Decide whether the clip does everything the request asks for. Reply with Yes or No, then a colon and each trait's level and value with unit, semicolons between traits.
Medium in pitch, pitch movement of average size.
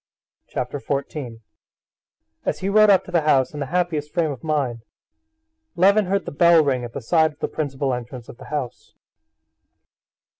Yes: medium, 150 Hz; average, 4.7 semitones